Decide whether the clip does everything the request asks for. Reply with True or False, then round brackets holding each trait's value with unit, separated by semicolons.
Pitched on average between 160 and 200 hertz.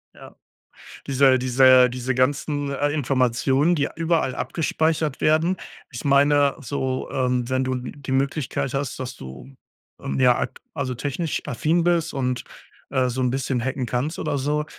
False (135 Hz)